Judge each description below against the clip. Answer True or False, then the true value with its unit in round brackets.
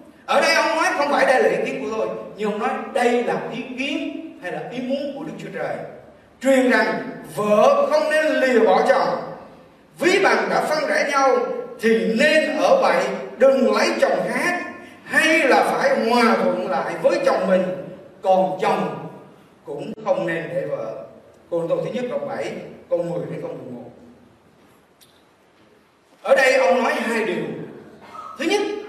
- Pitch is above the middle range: True (270 Hz)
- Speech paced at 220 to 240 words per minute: False (175 wpm)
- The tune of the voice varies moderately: True (4.4 semitones)